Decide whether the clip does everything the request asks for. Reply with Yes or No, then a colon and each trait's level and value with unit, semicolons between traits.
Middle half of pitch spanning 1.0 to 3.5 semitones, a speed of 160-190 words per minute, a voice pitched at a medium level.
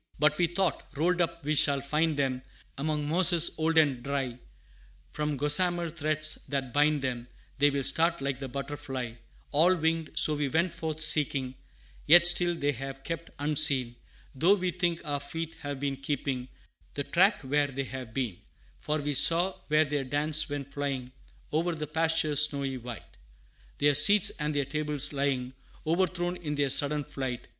Yes: average, 2.9 semitones; average, 165 wpm; medium, 150 Hz